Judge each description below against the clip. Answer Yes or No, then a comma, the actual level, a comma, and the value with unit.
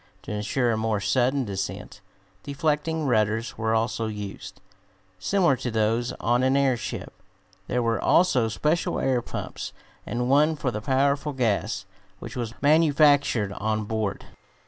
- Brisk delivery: No, average, 140 wpm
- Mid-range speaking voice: No, low, 120 Hz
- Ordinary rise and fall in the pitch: Yes, average, 4.4 semitones